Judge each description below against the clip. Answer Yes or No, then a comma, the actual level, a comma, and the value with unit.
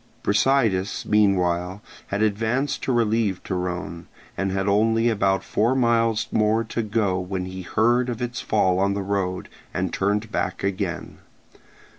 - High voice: No, low, 100 Hz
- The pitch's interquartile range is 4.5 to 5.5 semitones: No, average, 3.2 semitones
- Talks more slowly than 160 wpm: Yes, average, 145 wpm